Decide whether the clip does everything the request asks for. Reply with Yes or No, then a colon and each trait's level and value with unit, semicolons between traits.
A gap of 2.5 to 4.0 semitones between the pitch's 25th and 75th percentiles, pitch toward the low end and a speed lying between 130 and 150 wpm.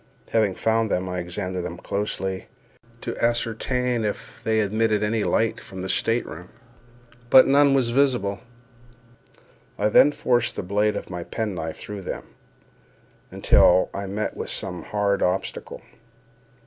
Yes: average, 3.4 semitones; low, 105 Hz; average, 145 wpm